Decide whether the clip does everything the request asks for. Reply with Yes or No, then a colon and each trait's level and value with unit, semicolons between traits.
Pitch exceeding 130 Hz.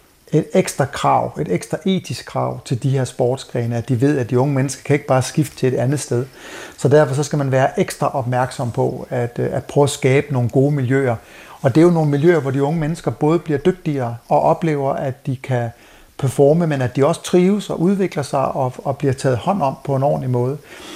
Yes: medium, 140 Hz